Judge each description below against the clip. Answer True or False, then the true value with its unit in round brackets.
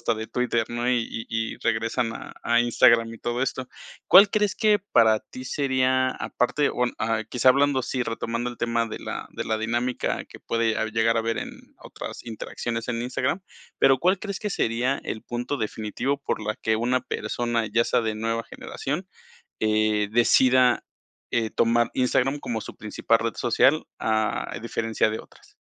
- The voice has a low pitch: True (120 Hz)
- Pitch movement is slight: True (2.3 semitones)